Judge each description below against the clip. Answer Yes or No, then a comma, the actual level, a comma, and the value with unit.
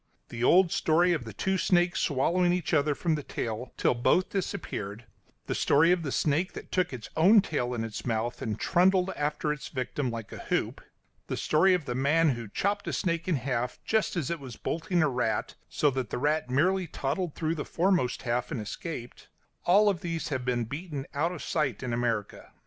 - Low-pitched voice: No, medium, 150 Hz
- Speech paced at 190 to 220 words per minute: Yes, fast, 205 wpm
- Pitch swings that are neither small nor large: No, wide, 6.0 semitones